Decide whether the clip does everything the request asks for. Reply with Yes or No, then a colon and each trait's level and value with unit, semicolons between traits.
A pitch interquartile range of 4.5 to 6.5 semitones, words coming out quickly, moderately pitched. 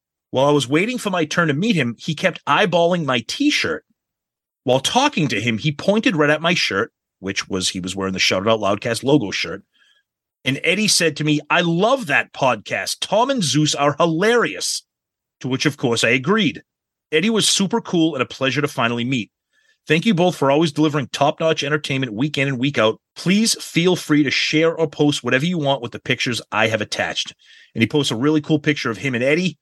Yes: average, 5.0 semitones; fast, 215 wpm; medium, 150 Hz